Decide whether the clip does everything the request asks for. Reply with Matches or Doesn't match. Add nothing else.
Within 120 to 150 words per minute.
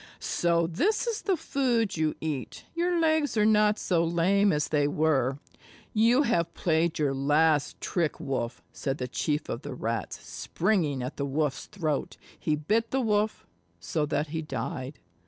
Doesn't match